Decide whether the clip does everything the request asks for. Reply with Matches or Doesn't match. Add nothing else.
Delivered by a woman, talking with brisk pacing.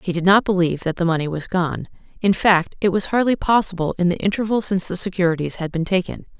Matches